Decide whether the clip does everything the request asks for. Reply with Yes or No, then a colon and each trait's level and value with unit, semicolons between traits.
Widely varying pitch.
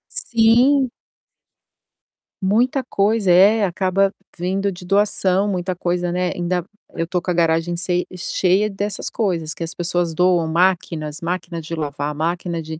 No: average, 2.7 semitones